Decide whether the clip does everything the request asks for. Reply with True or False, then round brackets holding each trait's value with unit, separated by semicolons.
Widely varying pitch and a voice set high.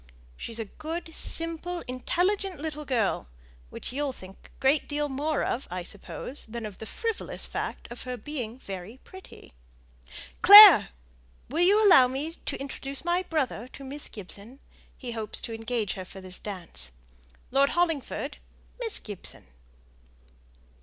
True (6.5 semitones; 270 Hz)